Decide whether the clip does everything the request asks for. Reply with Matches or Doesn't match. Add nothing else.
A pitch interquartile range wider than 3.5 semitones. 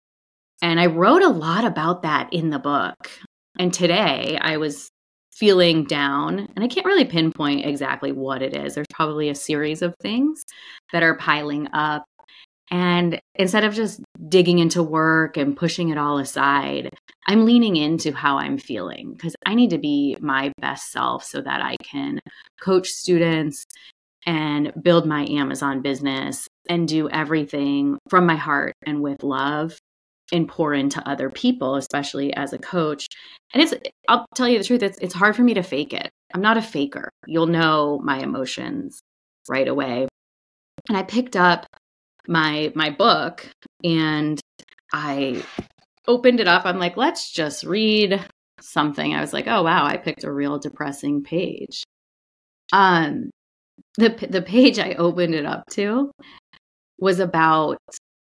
Matches